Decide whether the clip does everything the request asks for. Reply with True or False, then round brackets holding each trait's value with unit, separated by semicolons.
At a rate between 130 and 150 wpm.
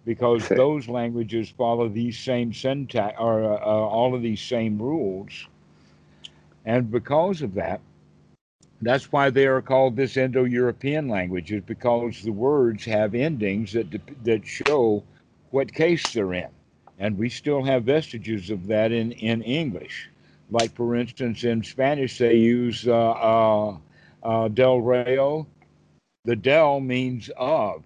True (140 wpm)